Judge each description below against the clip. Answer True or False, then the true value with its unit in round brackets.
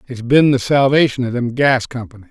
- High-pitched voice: False (125 Hz)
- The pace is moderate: False (210 wpm)